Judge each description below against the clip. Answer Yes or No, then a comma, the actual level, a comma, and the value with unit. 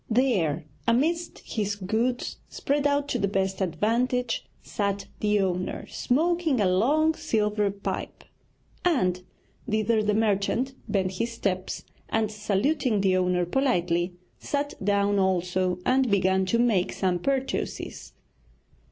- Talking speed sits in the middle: No, slow, 125 wpm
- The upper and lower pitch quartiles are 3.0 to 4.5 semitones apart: No, average, 4.9 semitones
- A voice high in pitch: Yes, high, 210 Hz